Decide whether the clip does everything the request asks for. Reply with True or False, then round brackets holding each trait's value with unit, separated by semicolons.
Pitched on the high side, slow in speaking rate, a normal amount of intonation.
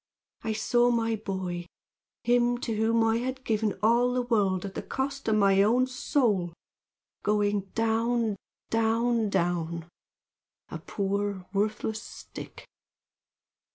True (220 Hz; 120 wpm; 3.2 semitones)